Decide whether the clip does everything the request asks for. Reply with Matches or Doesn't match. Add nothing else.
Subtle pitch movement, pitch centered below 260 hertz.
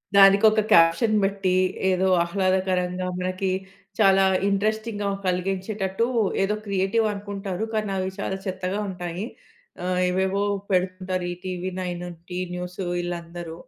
Matches